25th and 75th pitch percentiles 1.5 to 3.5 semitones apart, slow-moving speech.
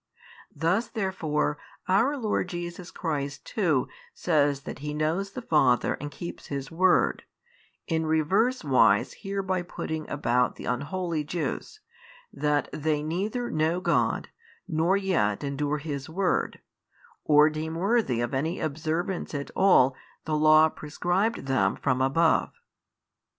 No: average, 4.0 semitones; slow, 130 wpm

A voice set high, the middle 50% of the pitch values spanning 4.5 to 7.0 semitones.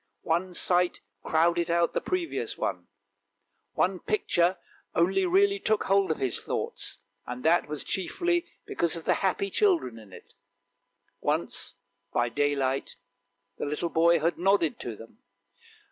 No: medium, 170 Hz; average, 4.8 semitones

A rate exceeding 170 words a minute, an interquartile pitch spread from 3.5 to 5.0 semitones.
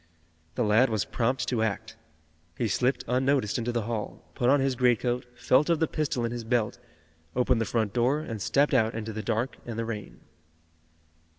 No: average, 190 wpm; narrow, 2.4 semitones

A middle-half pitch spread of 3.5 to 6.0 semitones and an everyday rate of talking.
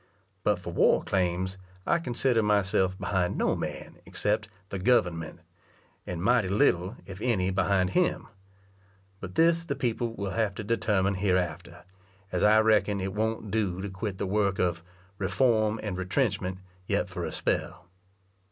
No: average, 3.1 semitones; average, 150 wpm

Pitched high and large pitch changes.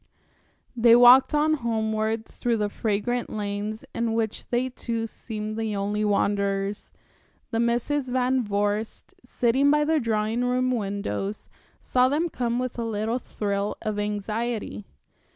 No: high, 225 Hz; average, 2.9 semitones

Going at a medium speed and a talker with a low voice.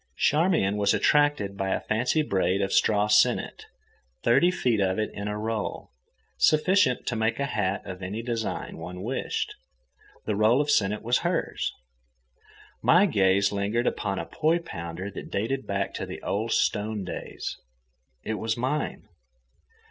Yes: average, 155 wpm; low, 110 Hz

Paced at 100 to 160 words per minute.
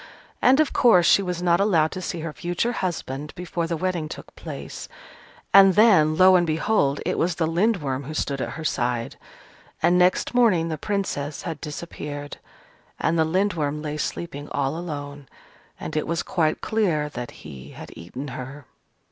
No: average, 175 wpm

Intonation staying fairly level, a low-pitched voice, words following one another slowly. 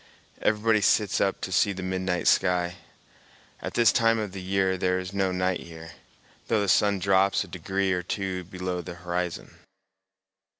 No: narrow, 1.6 semitones; very low, 95 Hz; average, 170 wpm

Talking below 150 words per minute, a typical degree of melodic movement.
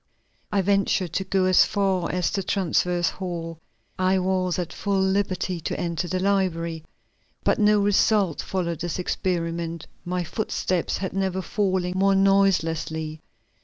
No: average, 140 wpm; narrow, 2.2 semitones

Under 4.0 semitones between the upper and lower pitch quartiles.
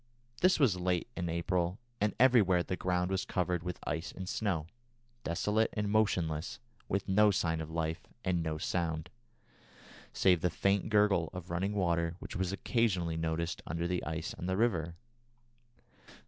Yes: average, 2.9 semitones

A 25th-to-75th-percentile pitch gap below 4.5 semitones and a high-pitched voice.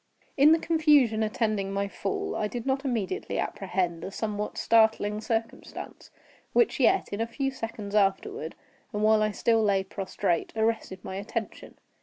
Yes: average, 2.7 semitones; high, 215 Hz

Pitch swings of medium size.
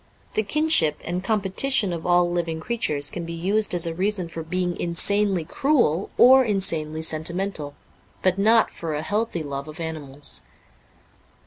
Yes: average, 4.3 semitones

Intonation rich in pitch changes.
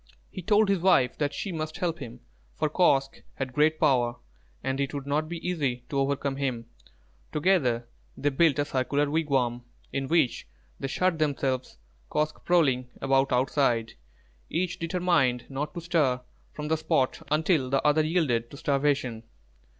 No: average, 3.4 semitones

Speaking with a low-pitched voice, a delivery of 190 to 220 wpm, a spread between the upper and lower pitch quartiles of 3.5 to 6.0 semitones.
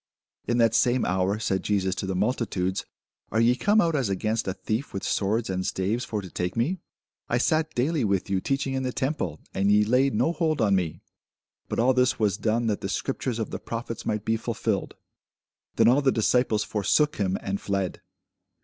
Yes: low, 110 Hz; fast, 205 wpm; average, 4.5 semitones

